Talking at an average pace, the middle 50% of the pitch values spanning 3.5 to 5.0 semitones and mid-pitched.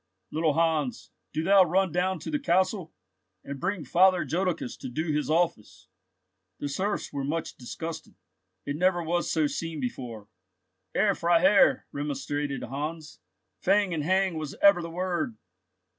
Yes: average, 145 wpm; average, 4.0 semitones; medium, 165 Hz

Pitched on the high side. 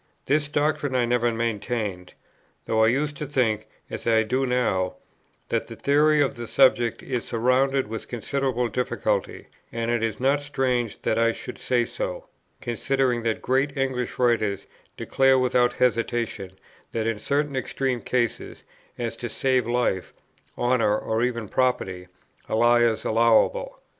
No: low, 120 Hz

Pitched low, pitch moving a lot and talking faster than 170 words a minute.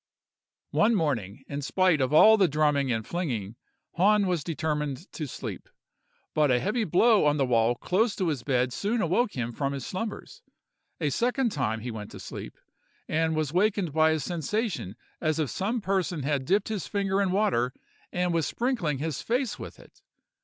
No: medium, 160 Hz; wide, 6.4 semitones; average, 180 wpm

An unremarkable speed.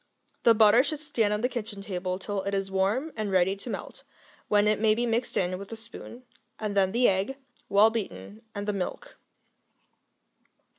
Yes: average, 190 wpm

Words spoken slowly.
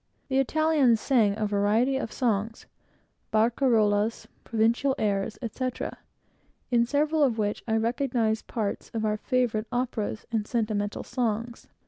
Yes: slow, 125 wpm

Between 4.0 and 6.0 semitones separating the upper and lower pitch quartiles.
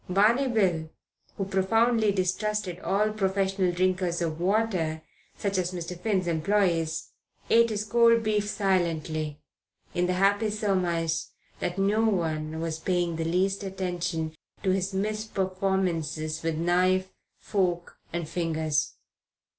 No: average, 3.3 semitones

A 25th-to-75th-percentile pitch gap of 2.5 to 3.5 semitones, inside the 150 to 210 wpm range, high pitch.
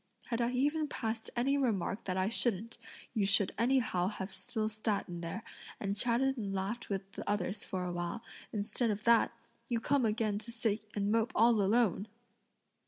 Yes: average, 3.2 semitones; average, 180 wpm; high, 215 Hz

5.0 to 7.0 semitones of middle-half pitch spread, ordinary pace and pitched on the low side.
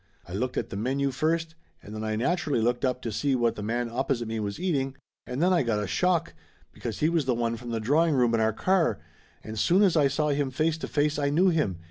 No: average, 5.3 semitones; fast, 255 wpm; low, 130 Hz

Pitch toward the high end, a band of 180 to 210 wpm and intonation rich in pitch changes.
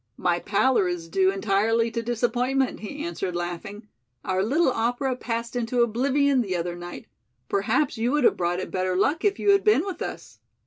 Yes: high, 230 Hz; average, 185 wpm; wide, 5.8 semitones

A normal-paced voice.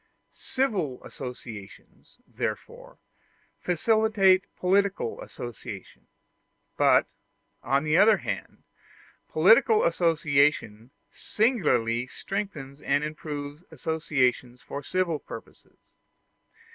No: slow, 75 wpm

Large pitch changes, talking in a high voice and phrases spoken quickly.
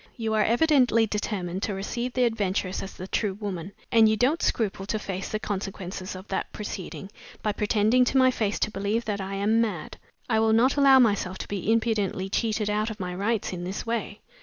No: average, 2.8 semitones; high, 210 Hz; fast, 210 wpm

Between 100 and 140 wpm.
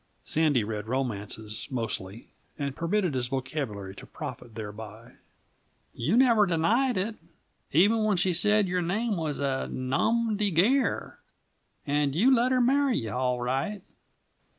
Yes: slow, 135 wpm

